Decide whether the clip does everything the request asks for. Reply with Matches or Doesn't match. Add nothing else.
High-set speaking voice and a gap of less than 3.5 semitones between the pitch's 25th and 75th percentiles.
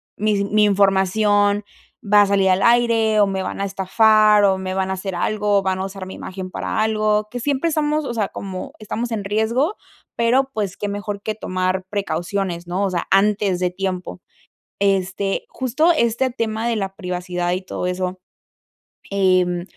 Matches